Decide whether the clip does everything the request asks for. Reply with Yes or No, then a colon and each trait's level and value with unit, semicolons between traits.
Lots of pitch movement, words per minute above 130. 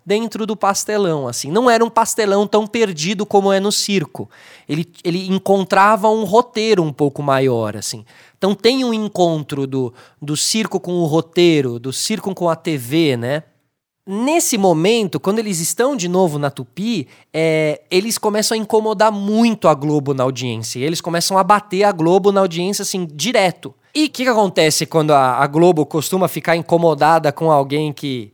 Yes: wide, 5.9 semitones; average, 175 wpm